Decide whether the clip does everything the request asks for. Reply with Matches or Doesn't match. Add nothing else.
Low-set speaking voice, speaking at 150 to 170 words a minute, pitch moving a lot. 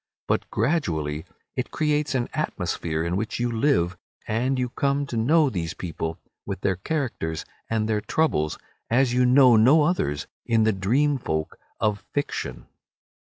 Matches